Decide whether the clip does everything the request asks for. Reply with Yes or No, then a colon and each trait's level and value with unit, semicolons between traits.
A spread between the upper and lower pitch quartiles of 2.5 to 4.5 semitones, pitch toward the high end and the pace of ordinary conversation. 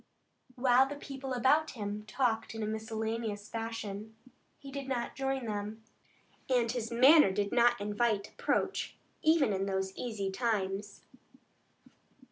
No: average, 3.7 semitones; high, 225 Hz; slow, 130 wpm